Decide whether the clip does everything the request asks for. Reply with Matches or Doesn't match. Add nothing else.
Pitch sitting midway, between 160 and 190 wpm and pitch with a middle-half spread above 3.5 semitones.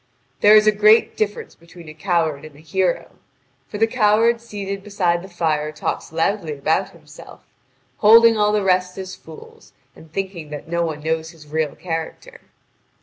Matches